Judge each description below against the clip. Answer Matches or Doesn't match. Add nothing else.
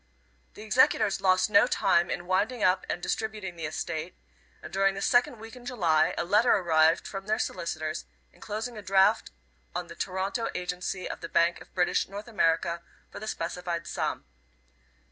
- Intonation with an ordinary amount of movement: Matches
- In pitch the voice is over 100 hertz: Matches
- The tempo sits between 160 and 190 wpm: Matches